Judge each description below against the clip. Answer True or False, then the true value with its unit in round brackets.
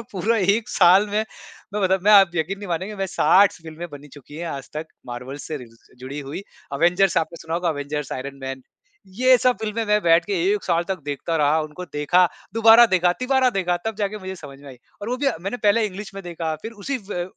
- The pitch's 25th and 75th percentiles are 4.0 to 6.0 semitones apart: True (5.3 semitones)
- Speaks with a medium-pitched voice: True (180 Hz)